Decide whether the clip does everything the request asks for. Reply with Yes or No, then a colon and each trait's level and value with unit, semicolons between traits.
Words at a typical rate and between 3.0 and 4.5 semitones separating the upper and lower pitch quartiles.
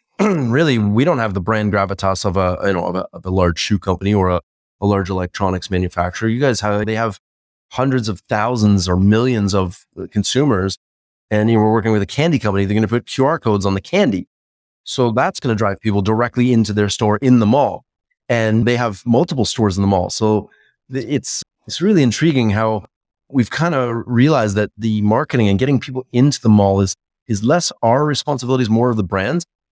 No: fast, 210 wpm; average, 4.0 semitones